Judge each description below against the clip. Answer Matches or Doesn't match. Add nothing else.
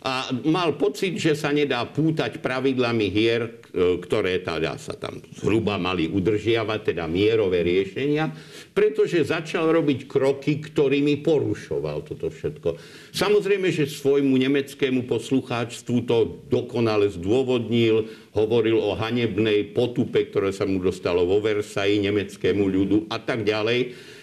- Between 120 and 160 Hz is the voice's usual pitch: Matches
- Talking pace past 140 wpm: Doesn't match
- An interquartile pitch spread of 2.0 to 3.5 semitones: Doesn't match